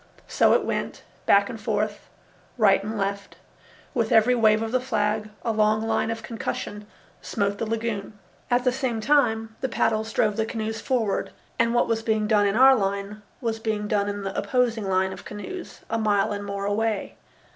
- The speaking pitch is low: No, high, 220 Hz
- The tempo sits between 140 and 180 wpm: No, average, 190 wpm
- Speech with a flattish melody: Yes, narrow, 1.8 semitones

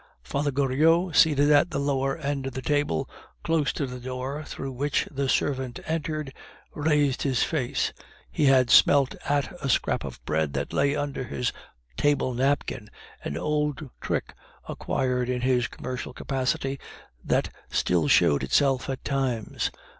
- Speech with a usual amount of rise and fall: No, narrow, 2.3 semitones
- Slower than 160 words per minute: Yes, average, 150 wpm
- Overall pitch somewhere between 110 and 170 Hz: Yes, low, 135 Hz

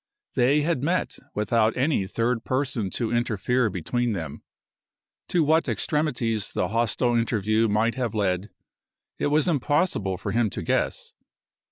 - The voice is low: Yes, low, 120 Hz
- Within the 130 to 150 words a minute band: Yes, average, 140 wpm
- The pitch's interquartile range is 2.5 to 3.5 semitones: No, average, 4.3 semitones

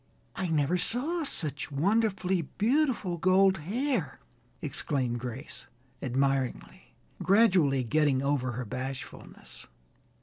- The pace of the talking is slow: Yes, slow, 95 wpm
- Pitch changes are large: Yes, wide, 6.5 semitones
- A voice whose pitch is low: No, medium, 155 Hz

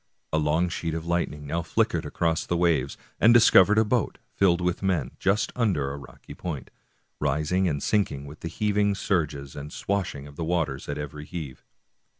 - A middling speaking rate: Yes, average, 180 wpm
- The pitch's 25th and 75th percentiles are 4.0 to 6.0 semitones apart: Yes, average, 4.6 semitones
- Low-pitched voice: Yes, very low, 85 Hz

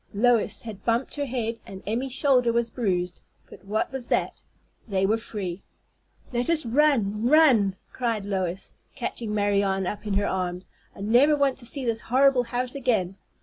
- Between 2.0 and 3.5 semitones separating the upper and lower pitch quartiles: No, average, 4.2 semitones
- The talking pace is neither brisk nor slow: Yes, average, 170 wpm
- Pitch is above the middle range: Yes, high, 230 Hz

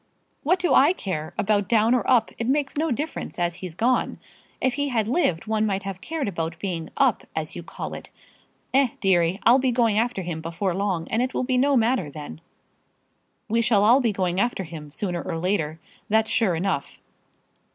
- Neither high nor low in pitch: No, high, 210 Hz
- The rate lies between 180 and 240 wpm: Yes, average, 200 wpm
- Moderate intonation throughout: No, wide, 6.1 semitones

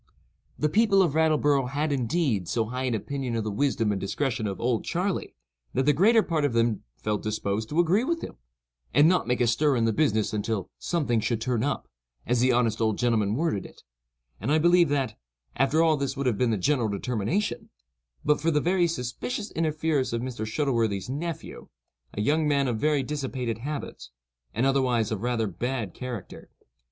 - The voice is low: Yes, low, 130 Hz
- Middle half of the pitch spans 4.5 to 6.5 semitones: Yes, average, 5.2 semitones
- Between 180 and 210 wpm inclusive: Yes, average, 190 wpm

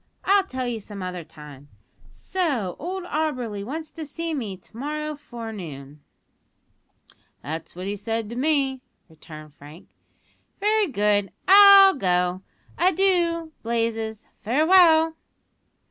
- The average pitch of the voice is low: No, high, 240 Hz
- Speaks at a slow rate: Yes, slow, 115 wpm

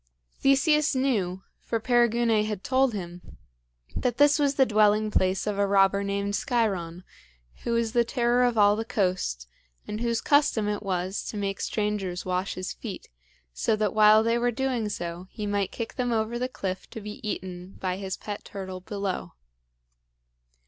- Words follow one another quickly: No, average, 170 wpm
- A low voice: No, high, 210 Hz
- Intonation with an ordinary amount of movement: Yes, average, 3.7 semitones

